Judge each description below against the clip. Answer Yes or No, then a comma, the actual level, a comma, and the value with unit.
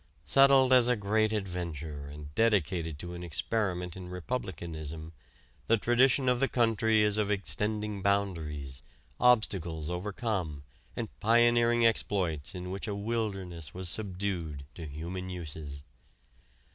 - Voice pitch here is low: Yes, very low, 95 Hz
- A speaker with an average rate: No, slow, 125 wpm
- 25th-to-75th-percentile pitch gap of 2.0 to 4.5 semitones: No, average, 5.1 semitones